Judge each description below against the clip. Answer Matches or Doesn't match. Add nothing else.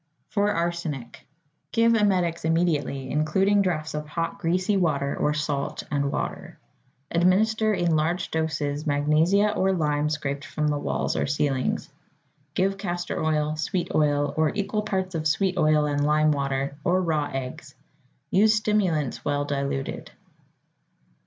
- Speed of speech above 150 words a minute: Doesn't match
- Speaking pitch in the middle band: Matches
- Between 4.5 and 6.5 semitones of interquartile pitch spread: Doesn't match